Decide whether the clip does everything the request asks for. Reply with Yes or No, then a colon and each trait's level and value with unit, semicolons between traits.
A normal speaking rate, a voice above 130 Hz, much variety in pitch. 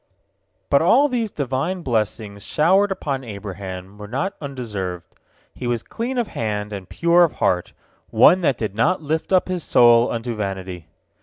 No: average, 160 wpm; low, 120 Hz; wide, 8.9 semitones